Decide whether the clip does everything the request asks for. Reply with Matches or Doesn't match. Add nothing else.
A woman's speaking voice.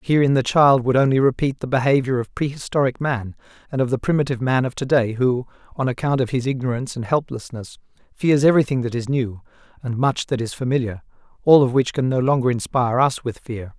Doesn't match